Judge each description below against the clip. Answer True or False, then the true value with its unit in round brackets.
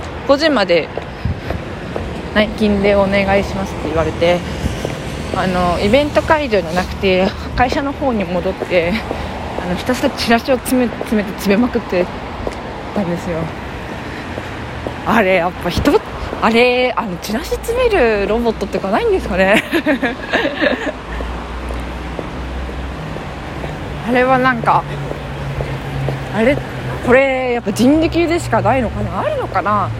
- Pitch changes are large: True (6.5 semitones)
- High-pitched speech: True (215 Hz)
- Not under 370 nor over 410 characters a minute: False (250 characters per minute)